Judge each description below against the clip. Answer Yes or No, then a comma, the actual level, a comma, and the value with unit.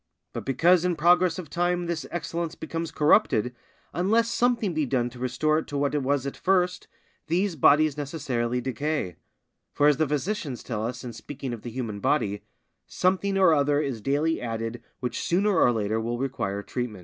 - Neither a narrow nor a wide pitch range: No, wide, 5.8 semitones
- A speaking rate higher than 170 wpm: Yes, average, 185 wpm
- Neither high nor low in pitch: Yes, medium, 145 Hz